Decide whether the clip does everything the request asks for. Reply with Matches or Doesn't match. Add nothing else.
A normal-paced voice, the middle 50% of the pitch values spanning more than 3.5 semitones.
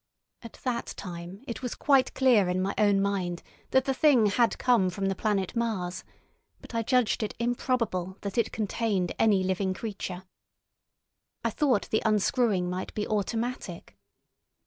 Matches